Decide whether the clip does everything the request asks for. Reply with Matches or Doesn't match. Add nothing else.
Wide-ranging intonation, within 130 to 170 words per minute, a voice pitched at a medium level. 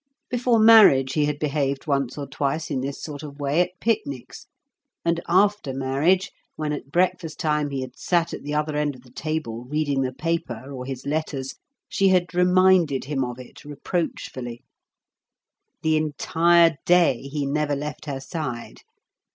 Doesn't match